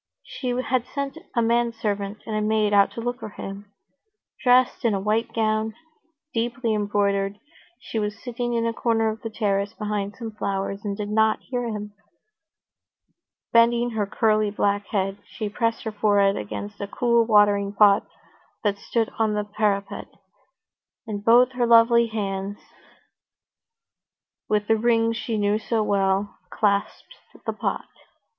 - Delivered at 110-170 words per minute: Yes, average, 150 wpm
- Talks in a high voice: Yes, high, 215 Hz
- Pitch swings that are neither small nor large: No, narrow, 2.2 semitones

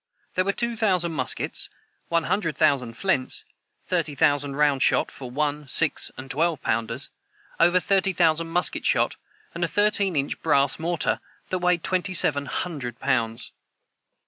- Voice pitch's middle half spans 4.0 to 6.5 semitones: Yes, average, 4.4 semitones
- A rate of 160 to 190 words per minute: No, average, 150 wpm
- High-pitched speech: No, medium, 160 Hz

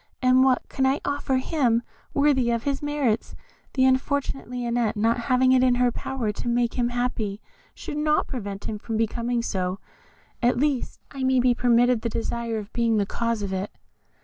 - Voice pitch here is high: Yes, high, 245 Hz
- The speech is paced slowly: No, average, 185 wpm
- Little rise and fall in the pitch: Yes, narrow, 2.3 semitones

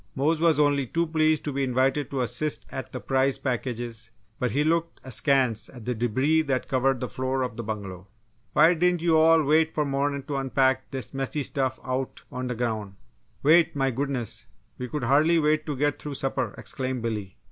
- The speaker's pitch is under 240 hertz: Yes, low, 135 Hz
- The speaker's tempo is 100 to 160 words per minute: No, average, 195 wpm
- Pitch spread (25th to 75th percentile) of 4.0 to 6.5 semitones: No, average, 3.3 semitones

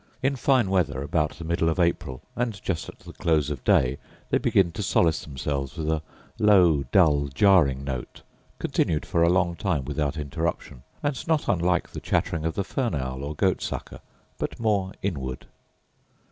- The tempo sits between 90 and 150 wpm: No, average, 175 wpm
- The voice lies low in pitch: Yes, very low, 80 Hz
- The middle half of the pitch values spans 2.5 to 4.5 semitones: No, average, 4.9 semitones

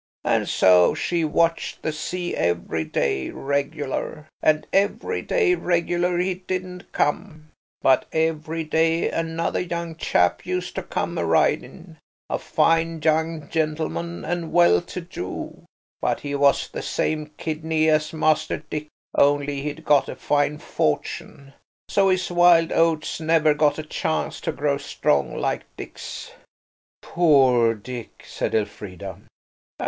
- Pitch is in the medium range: Yes, medium, 155 Hz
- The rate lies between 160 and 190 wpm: No, slow, 135 wpm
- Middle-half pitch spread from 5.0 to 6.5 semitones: No, average, 2.8 semitones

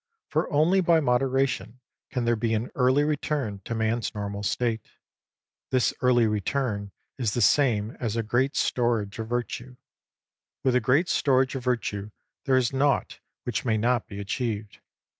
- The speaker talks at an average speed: Yes, average, 160 wpm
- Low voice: Yes, low, 120 Hz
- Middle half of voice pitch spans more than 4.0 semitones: No, average, 3.2 semitones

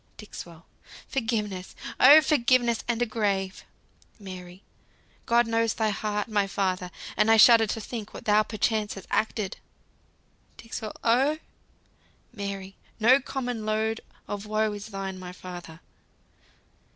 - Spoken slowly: Yes, slow, 125 wpm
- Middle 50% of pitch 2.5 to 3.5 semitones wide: Yes, average, 2.8 semitones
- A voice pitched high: Yes, high, 215 Hz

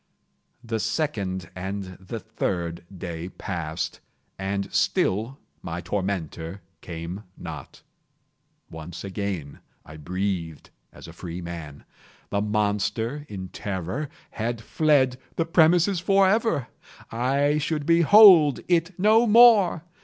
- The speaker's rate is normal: No, slow, 105 wpm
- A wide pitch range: Yes, wide, 9.0 semitones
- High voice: No, low, 105 Hz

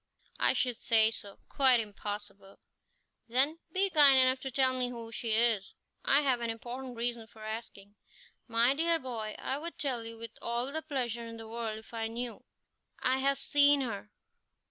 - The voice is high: Yes, high, 240 Hz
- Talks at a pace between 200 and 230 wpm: No, average, 180 wpm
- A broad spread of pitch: No, average, 2.9 semitones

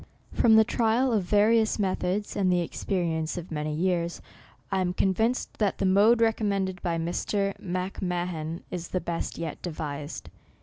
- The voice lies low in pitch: No, medium, 185 Hz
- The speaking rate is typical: Yes, average, 155 wpm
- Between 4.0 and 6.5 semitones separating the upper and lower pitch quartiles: No, average, 3.4 semitones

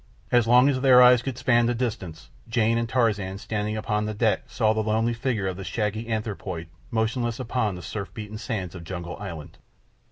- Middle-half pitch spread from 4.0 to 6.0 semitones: No, average, 3.2 semitones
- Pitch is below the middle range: Yes, low, 110 Hz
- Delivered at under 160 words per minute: No, average, 200 wpm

